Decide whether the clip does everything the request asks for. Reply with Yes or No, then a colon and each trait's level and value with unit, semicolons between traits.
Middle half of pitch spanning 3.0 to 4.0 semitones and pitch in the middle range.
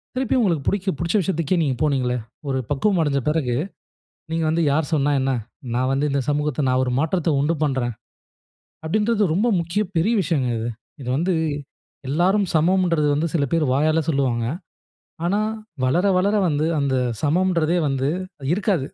No: average, 4.6 semitones; medium, 155 Hz